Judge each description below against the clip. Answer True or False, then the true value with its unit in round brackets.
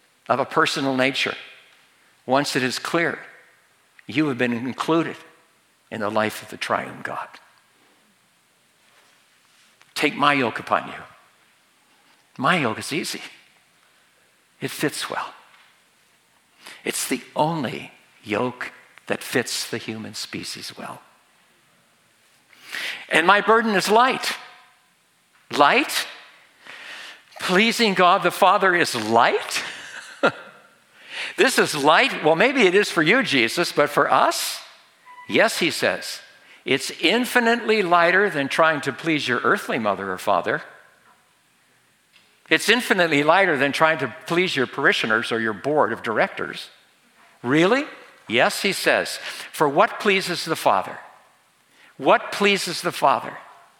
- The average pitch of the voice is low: False (160 Hz)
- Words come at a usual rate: False (120 wpm)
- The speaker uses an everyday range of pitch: False (7.3 semitones)